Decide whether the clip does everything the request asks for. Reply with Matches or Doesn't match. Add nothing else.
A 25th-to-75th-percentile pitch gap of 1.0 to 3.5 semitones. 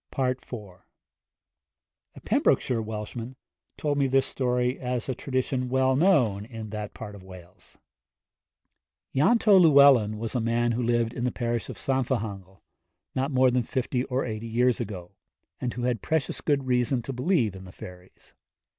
Matches